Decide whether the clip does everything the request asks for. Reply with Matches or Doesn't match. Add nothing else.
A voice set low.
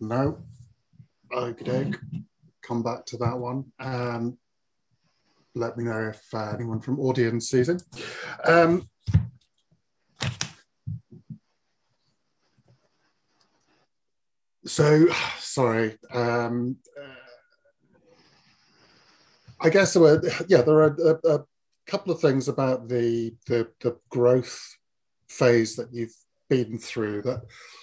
Matches